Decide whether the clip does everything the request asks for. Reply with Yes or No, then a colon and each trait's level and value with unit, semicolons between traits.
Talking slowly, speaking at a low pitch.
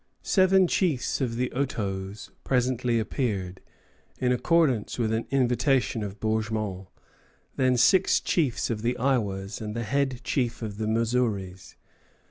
Yes: slow, 130 wpm; low, 120 Hz